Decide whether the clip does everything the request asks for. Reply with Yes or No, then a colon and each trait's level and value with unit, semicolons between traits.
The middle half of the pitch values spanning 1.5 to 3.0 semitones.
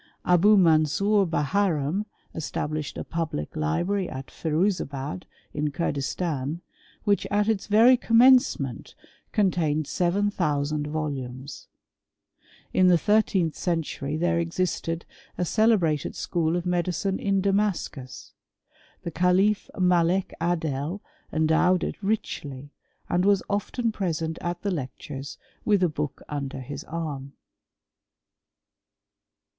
No: average, 4.7 semitones